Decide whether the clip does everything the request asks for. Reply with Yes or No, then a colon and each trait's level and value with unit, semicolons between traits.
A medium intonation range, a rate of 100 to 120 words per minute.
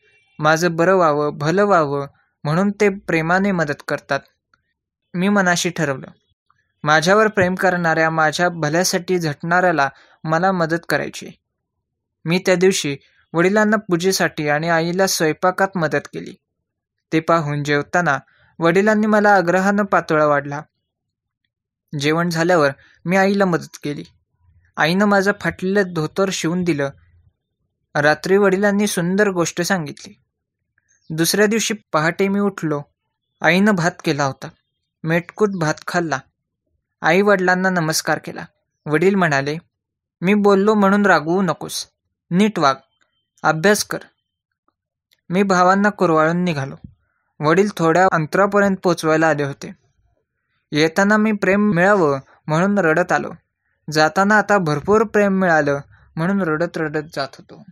Yes: average, 4.5 semitones; average, 115 wpm